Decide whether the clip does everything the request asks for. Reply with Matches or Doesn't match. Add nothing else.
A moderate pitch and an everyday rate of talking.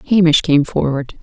Matches